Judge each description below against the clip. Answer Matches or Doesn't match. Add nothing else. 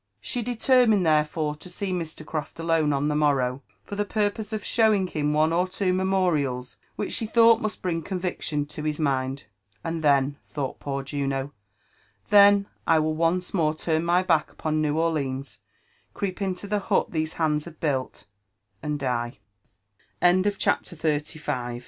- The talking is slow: Doesn't match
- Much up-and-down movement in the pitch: Doesn't match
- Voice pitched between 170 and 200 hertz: Doesn't match